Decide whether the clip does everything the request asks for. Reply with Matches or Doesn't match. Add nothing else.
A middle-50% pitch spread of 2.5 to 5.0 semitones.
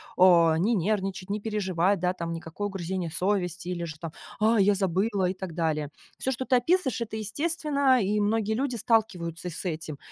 Matches